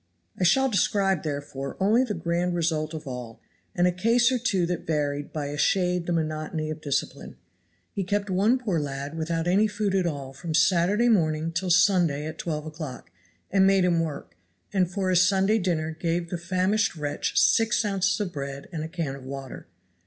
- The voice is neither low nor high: Yes, medium, 170 Hz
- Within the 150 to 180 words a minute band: No, average, 190 wpm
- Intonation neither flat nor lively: Yes, average, 3.9 semitones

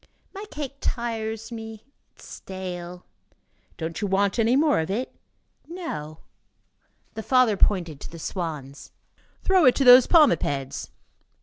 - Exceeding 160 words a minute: No, slow, 135 wpm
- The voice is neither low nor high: No, high, 220 Hz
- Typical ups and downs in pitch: No, wide, 6.7 semitones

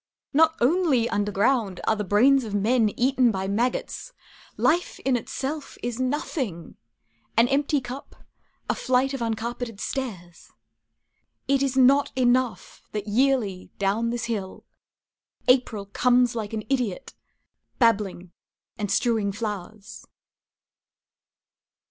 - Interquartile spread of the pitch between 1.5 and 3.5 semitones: No, average, 4.1 semitones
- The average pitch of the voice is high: Yes, high, 235 Hz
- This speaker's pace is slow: Yes, slow, 120 wpm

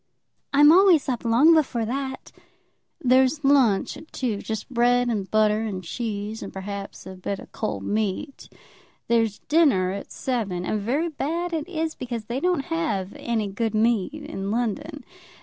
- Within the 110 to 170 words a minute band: Yes, average, 160 wpm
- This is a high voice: Yes, high, 235 Hz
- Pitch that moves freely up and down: Yes, wide, 5.7 semitones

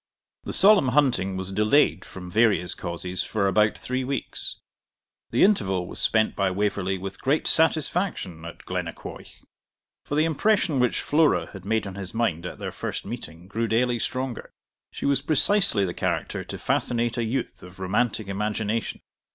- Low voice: Yes, low, 110 Hz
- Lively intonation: Yes, wide, 5.8 semitones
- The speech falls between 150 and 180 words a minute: Yes, average, 160 wpm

